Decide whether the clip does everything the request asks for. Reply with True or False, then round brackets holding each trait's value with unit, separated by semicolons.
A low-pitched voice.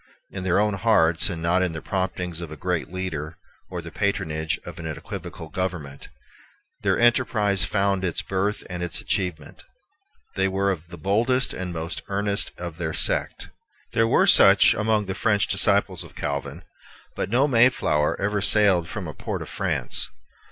True (95 Hz)